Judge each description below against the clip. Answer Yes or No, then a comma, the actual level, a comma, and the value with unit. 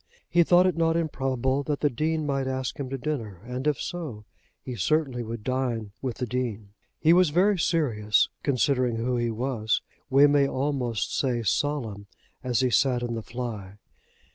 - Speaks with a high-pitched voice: No, low, 130 Hz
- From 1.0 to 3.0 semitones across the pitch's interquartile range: No, average, 3.9 semitones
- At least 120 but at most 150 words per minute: No, average, 175 wpm